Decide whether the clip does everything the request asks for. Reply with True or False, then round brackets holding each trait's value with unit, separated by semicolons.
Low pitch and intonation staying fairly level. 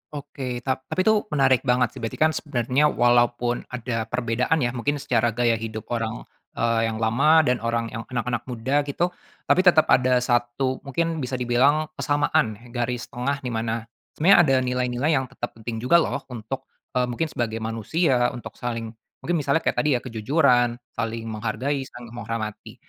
False (125 Hz; 3.2 semitones)